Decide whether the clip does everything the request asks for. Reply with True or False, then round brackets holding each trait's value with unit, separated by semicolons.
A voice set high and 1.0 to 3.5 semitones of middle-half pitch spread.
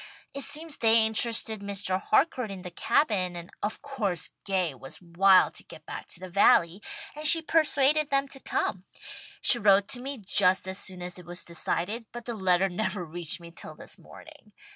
False (200 Hz; 5.4 semitones)